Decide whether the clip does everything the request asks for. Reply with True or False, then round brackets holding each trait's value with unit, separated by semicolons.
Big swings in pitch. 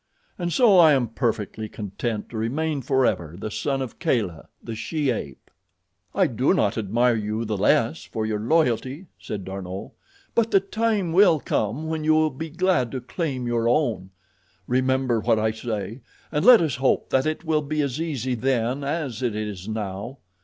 True (6.0 semitones)